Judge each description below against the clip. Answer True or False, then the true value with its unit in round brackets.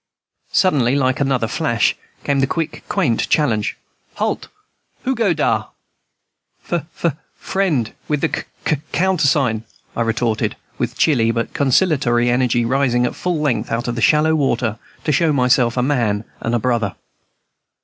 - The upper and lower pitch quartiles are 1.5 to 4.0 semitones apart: False (4.5 semitones)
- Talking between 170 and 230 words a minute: False (150 wpm)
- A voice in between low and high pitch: False (130 Hz)